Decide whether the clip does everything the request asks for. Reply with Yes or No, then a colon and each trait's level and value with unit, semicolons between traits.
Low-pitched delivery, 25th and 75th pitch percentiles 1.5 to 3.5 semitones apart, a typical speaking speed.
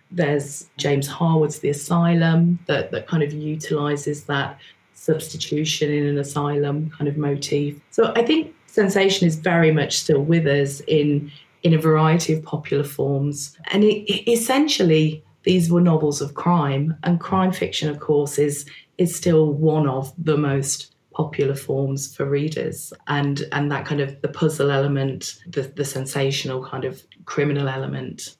No: medium, 150 Hz; average, 2.7 semitones; average, 160 wpm